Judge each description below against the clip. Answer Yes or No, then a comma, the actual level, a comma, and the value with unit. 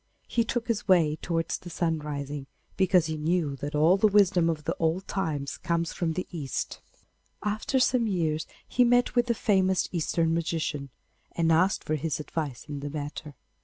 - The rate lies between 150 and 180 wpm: Yes, average, 175 wpm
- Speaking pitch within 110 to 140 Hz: No, medium, 165 Hz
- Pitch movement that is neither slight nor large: Yes, average, 3.9 semitones